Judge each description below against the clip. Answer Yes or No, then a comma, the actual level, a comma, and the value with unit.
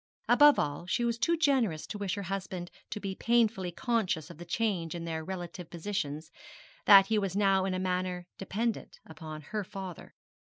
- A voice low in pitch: No, high, 190 Hz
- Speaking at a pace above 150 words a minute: Yes, average, 180 wpm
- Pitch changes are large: No, average, 3.5 semitones